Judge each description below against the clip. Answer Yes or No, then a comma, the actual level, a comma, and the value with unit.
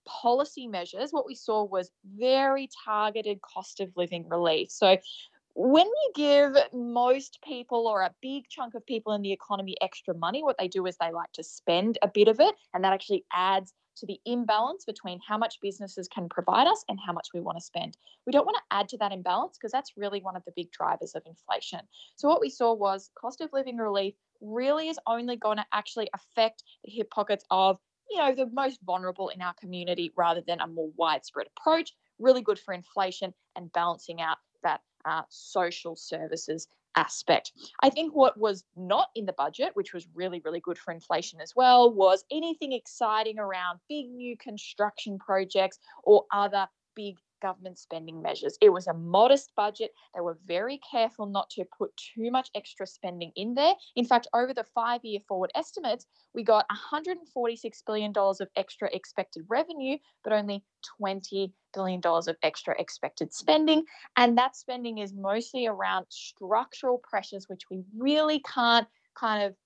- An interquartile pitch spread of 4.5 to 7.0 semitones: Yes, average, 5.2 semitones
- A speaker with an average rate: Yes, average, 185 wpm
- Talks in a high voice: Yes, high, 210 Hz